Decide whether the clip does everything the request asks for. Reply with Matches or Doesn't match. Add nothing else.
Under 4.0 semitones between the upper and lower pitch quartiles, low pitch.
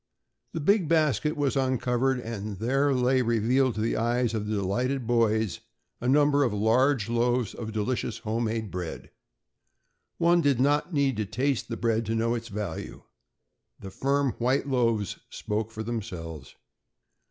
Matches